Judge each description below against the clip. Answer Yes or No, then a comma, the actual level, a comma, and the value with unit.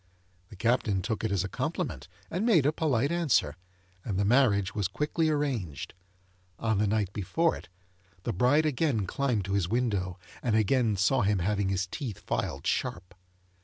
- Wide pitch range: Yes, wide, 5.9 semitones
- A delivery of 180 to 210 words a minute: No, average, 170 wpm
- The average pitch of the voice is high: No, low, 110 Hz